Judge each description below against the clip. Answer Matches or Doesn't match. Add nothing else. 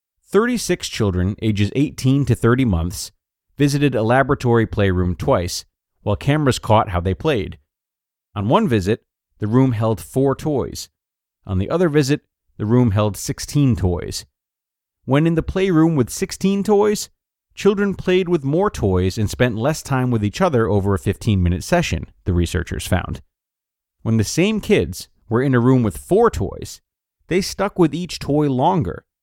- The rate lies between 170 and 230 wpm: Doesn't match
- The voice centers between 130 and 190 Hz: Doesn't match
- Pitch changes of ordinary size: Doesn't match